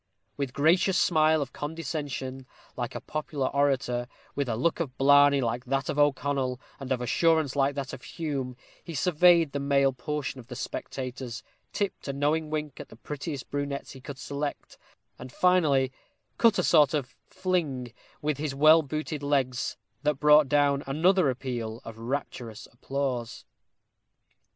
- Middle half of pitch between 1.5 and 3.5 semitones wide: Yes, average, 2.8 semitones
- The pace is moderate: Yes, average, 160 wpm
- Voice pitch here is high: No, medium, 140 Hz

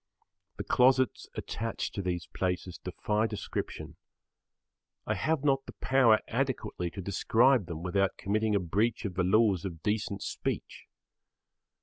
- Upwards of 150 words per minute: No, slow, 135 wpm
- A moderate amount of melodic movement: Yes, average, 4.2 semitones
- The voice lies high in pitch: No, low, 105 Hz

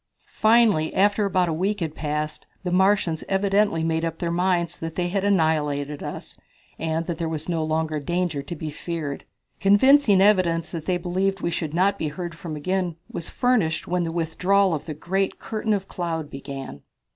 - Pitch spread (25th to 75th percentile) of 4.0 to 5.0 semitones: No, average, 3.3 semitones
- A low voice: No, medium, 170 Hz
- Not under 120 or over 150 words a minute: No, average, 185 wpm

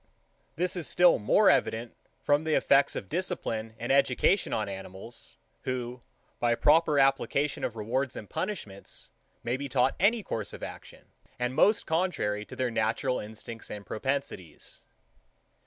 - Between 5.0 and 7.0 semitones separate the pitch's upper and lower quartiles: Yes, average, 5.3 semitones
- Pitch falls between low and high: No, low, 125 Hz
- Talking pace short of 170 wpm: Yes, average, 150 wpm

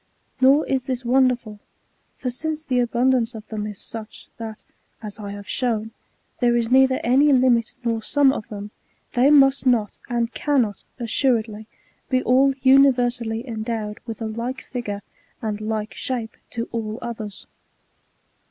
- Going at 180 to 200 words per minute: No, average, 155 wpm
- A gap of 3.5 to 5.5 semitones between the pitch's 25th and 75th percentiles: No, average, 2.9 semitones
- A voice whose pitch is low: No, high, 235 Hz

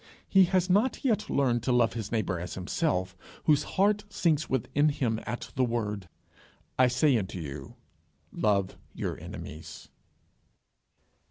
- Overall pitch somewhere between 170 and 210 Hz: No, low, 120 Hz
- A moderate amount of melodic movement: No, wide, 8.0 semitones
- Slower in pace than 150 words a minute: Yes, average, 140 wpm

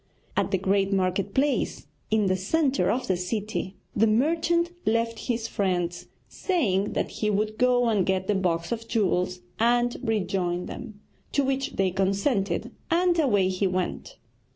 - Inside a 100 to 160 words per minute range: Yes, average, 155 wpm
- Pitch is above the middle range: Yes, high, 210 Hz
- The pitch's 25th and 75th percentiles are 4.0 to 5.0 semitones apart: Yes, average, 4.5 semitones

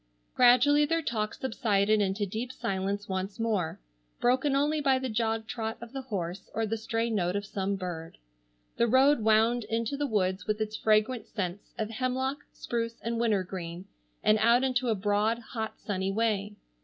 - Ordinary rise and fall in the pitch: Yes, average, 3.3 semitones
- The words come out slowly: No, average, 170 wpm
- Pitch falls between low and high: No, high, 220 Hz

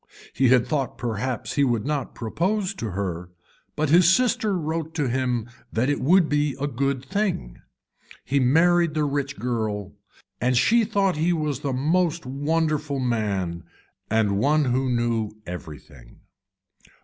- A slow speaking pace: No, average, 150 wpm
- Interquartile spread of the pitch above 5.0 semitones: Yes, wide, 5.4 semitones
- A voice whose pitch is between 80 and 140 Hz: Yes, low, 135 Hz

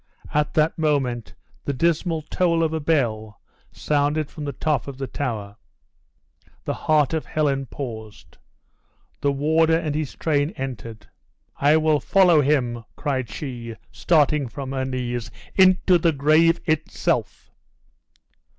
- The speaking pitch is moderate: Yes, medium, 145 Hz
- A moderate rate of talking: No, slow, 130 wpm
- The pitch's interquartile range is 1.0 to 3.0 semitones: No, average, 3.5 semitones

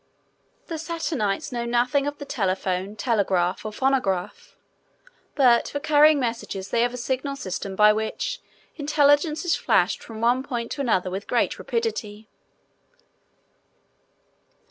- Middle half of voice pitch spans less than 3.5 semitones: No, wide, 5.6 semitones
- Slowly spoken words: Yes, slow, 130 wpm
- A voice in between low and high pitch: No, high, 240 Hz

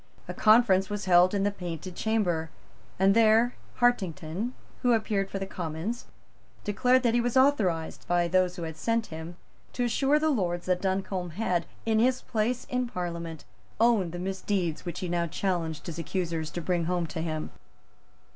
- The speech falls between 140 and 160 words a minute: No, average, 175 wpm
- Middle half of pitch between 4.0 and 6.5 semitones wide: Yes, average, 4.7 semitones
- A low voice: No, high, 190 Hz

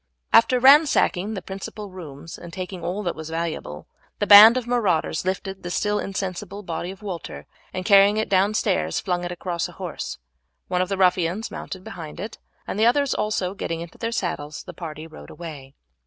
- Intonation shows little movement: No, average, 3.6 semitones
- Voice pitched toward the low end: No, medium, 185 Hz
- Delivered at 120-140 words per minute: No, average, 190 wpm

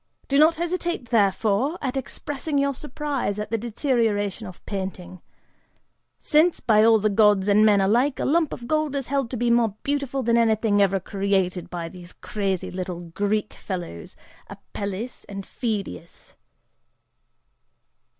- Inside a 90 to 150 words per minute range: Yes, average, 145 wpm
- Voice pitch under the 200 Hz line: No, high, 220 Hz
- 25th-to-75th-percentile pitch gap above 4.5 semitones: Yes, wide, 5.5 semitones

